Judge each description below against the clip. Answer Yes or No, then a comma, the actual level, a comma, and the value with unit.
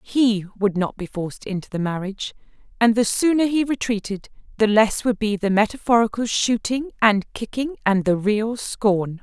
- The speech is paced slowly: No, average, 165 wpm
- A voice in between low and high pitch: No, high, 215 Hz